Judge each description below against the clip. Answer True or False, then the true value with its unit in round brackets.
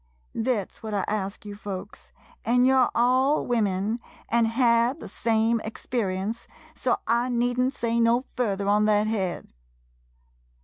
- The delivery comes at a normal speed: True (150 wpm)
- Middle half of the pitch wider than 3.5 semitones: False (2.8 semitones)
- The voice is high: True (230 Hz)